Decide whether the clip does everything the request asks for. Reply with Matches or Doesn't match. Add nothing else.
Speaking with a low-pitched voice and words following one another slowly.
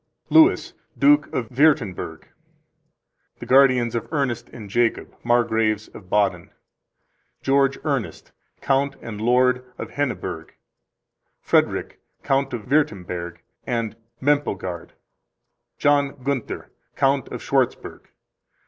Matches